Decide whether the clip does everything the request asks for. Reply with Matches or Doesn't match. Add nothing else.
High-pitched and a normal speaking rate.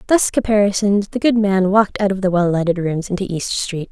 Doesn't match